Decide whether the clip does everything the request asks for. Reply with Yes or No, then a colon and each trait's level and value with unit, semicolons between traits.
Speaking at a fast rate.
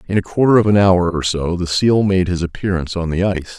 Yes: fast, 270 wpm